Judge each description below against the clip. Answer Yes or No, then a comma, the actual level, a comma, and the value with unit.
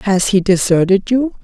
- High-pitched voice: Yes, high, 200 Hz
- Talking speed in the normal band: Yes, average, 165 wpm